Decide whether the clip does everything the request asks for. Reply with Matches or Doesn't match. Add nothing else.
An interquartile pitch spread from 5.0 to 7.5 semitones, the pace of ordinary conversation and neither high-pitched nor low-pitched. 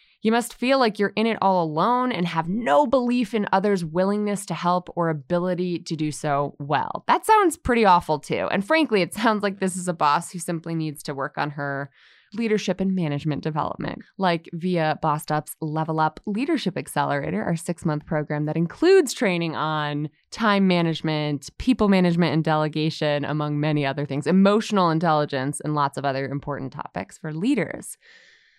Matches